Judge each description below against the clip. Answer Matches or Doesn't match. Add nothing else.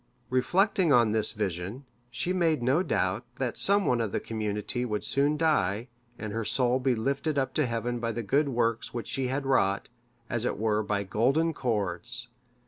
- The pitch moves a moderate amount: Matches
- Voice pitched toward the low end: Matches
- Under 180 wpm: Doesn't match